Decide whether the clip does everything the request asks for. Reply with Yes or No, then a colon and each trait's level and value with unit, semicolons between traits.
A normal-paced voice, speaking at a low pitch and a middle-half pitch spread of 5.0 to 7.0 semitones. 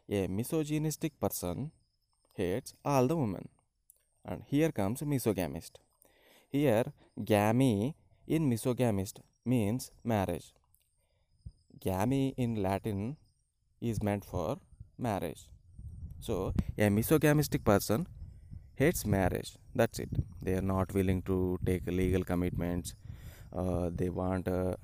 No: slow, 105 wpm; low, 100 Hz; wide, 5.5 semitones